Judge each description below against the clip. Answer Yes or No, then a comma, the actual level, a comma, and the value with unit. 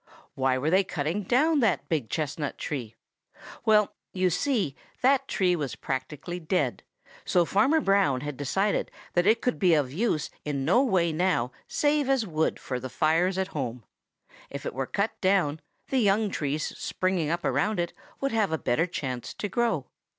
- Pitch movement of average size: No, wide, 6.2 semitones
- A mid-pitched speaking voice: Yes, medium, 175 Hz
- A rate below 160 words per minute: No, average, 175 wpm